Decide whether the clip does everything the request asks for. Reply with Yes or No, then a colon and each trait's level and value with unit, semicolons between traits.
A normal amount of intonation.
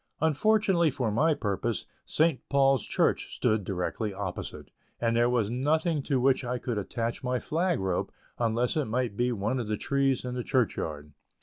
Yes: average, 4.2 semitones